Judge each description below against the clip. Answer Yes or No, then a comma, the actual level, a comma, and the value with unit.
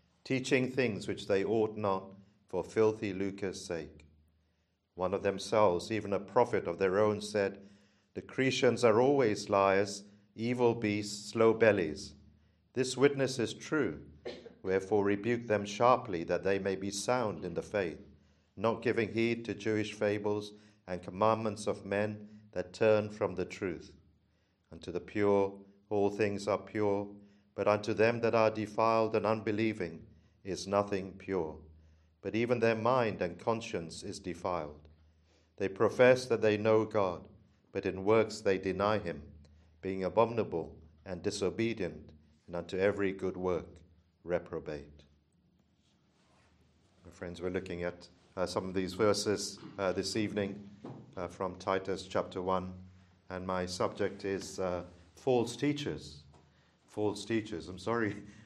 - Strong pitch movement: No, average, 3.2 semitones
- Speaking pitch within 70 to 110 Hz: Yes, low, 100 Hz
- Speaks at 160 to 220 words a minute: No, average, 140 wpm